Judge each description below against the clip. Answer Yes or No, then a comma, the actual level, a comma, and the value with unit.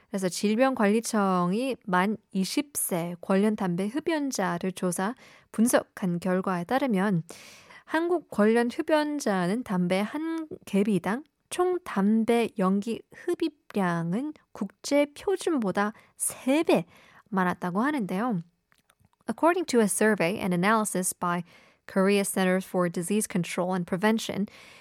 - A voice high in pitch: Yes, high, 210 Hz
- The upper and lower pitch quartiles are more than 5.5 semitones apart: Yes, wide, 6.2 semitones